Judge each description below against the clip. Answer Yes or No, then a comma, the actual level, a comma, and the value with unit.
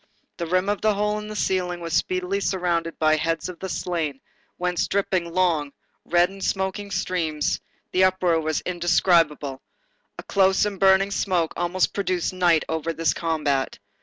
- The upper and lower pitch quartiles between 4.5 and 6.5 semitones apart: No, narrow, 2.5 semitones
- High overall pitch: No, medium, 180 Hz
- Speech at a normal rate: Yes, average, 165 wpm